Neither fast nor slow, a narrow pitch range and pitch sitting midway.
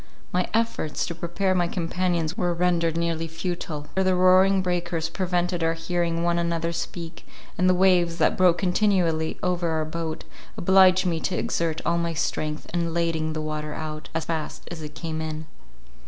Yes: average, 175 wpm; narrow, 1.8 semitones; medium, 170 Hz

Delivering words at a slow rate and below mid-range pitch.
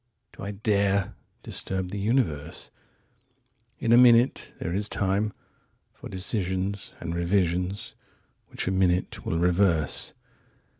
Yes: slow, 100 wpm; low, 100 Hz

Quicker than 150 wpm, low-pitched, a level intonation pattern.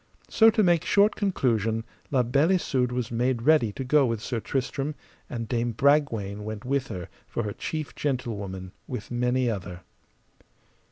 No: average, 160 wpm; low, 125 Hz; average, 4.2 semitones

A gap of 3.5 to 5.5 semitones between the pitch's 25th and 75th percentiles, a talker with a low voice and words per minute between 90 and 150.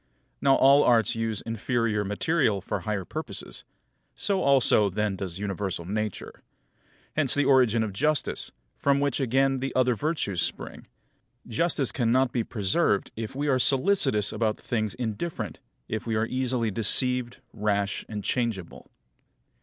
Yes: average, 4.3 semitones; low, 115 Hz; average, 140 wpm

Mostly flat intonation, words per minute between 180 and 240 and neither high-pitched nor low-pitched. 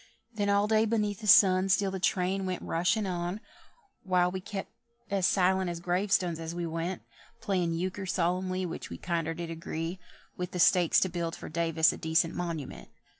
Yes: narrow, 2.3 semitones; average, 190 wpm; medium, 180 Hz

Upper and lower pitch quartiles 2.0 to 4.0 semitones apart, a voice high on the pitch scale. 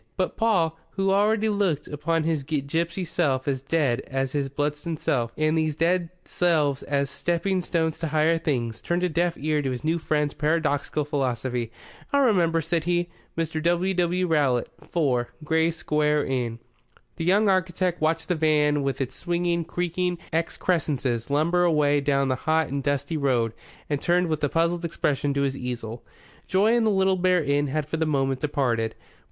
No: average, 3.5 semitones; medium, 155 Hz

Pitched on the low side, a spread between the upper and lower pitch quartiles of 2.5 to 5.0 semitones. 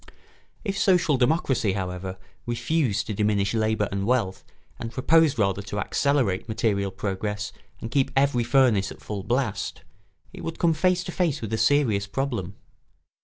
No: low, 115 Hz; wide, 5.5 semitones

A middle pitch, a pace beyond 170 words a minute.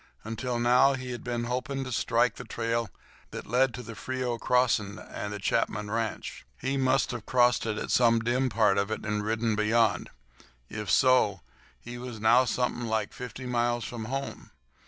No: low, 120 Hz; average, 180 wpm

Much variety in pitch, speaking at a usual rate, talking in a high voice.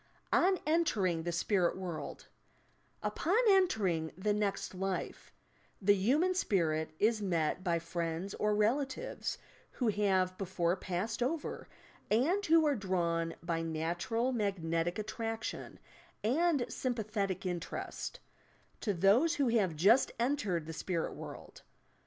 No: wide, 5.9 semitones; slow, 120 wpm; high, 200 Hz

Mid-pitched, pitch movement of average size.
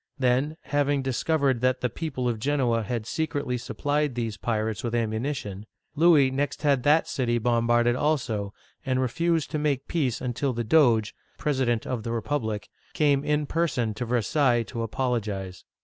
No: low, 125 Hz; average, 3.9 semitones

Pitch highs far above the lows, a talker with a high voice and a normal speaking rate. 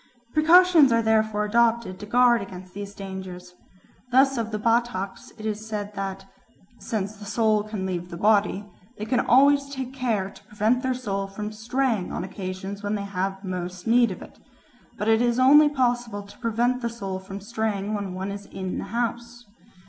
No: average, 3.4 semitones; high, 215 Hz; average, 180 wpm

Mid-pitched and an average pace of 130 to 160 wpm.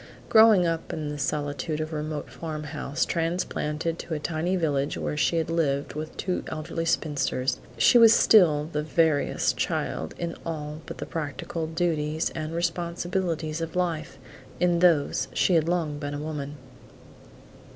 Yes: medium, 160 Hz; average, 155 wpm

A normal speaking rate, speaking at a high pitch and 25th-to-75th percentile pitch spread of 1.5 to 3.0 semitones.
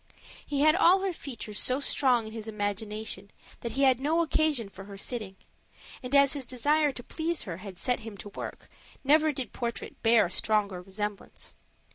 No: average, 185 wpm; high, 235 Hz; wide, 5.4 semitones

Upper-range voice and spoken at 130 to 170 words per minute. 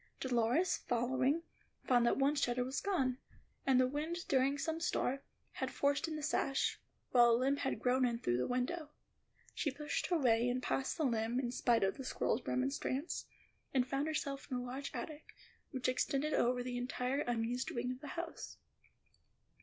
No: very high, 260 Hz; average, 185 wpm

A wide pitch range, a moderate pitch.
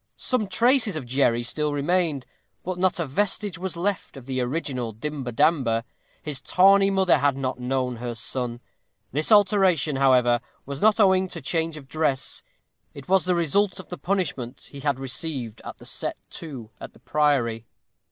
Yes: wide, 6.2 semitones; medium, 150 Hz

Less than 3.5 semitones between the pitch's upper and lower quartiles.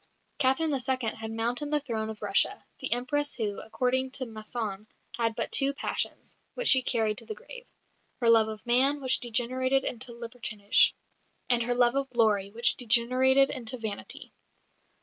Yes: average, 2.9 semitones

